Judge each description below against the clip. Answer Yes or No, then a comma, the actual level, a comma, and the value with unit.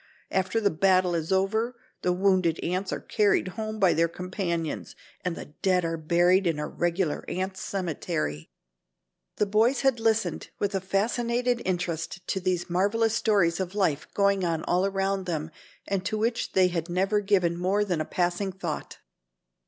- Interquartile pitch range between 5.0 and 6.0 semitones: No, average, 2.7 semitones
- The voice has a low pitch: No, medium, 185 Hz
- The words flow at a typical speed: Yes, average, 170 wpm